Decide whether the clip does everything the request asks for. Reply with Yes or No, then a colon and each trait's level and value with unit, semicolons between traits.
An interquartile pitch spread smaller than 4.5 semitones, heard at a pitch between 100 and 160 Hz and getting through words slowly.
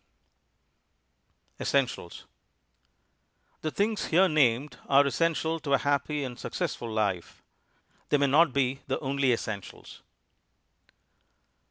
Yes: average, 3.5 semitones; medium, 140 Hz; slow, 110 wpm